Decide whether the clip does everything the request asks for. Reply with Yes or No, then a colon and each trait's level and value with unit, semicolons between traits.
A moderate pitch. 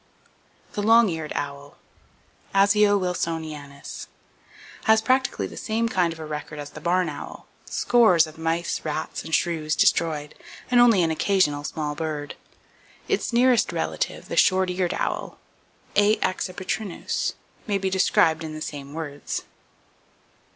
Yes: medium, 165 Hz